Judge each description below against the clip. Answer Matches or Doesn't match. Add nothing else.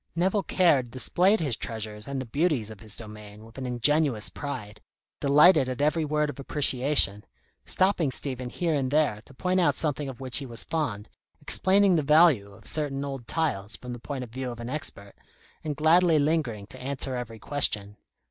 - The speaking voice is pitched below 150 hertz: Matches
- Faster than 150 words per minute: Matches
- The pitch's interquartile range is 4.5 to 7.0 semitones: Matches